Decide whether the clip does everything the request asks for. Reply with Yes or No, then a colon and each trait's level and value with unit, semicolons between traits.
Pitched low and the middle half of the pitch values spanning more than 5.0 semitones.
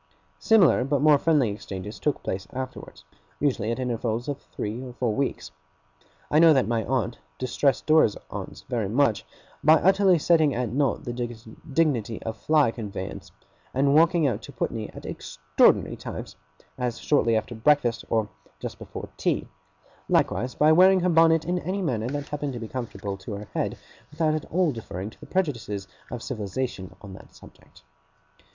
Yes: low, 125 Hz; wide, 5.4 semitones